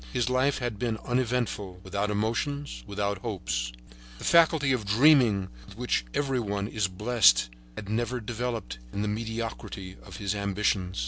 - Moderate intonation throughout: Yes, average, 3.6 semitones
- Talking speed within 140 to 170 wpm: Yes, average, 150 wpm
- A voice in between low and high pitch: No, low, 110 Hz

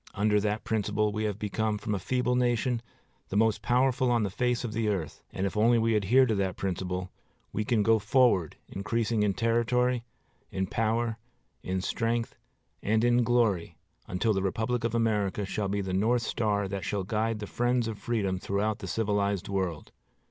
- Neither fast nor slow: Yes, average, 185 wpm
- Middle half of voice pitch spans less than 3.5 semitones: Yes, average, 2.9 semitones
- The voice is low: Yes, low, 110 Hz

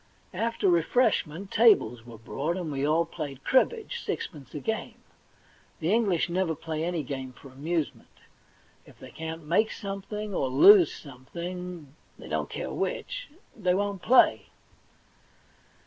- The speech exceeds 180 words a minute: No, average, 145 wpm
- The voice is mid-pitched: Yes, medium, 170 Hz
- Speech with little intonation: No, average, 5.3 semitones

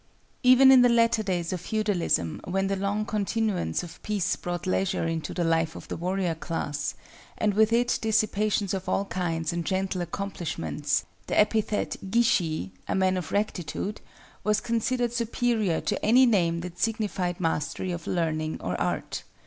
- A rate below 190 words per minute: Yes, average, 160 wpm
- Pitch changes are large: No, average, 4.3 semitones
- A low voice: No, high, 190 Hz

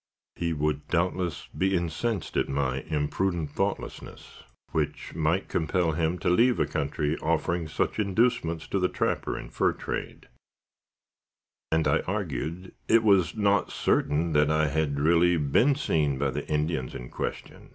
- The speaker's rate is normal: Yes, average, 150 wpm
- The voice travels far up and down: No, average, 3.7 semitones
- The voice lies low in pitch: Yes, very low, 80 Hz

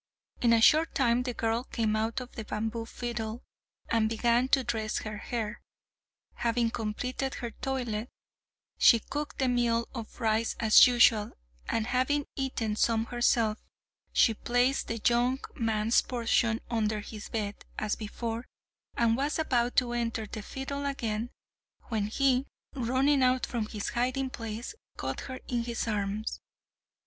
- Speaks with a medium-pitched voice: No, high, 235 Hz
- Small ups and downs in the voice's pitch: Yes, narrow, 2.3 semitones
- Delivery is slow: No, average, 150 wpm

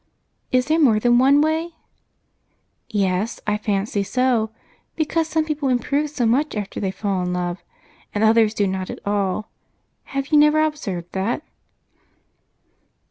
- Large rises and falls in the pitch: Yes, wide, 6.8 semitones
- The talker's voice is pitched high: Yes, high, 230 Hz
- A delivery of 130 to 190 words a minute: Yes, average, 145 wpm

